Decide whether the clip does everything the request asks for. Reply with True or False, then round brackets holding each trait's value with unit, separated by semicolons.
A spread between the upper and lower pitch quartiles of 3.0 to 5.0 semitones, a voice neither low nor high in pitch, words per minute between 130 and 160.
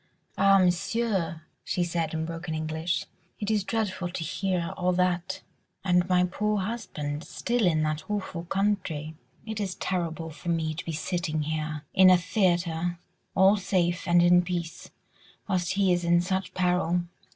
False (2.5 semitones; 175 Hz; 155 wpm)